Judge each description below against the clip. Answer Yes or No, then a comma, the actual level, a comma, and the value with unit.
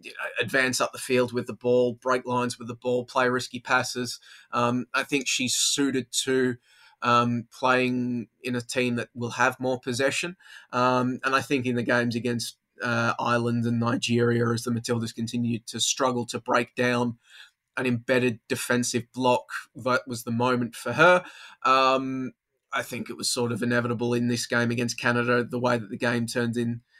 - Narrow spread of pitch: Yes, narrow, 1.1 semitones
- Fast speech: No, average, 180 wpm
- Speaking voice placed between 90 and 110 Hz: No, low, 120 Hz